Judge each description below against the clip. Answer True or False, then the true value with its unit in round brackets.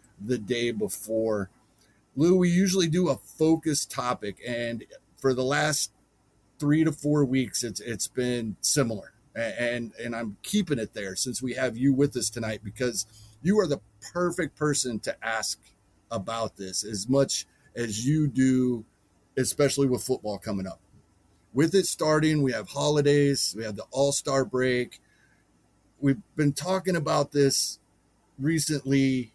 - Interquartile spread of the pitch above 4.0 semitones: True (4.8 semitones)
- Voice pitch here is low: True (130 Hz)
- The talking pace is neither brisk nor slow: True (145 wpm)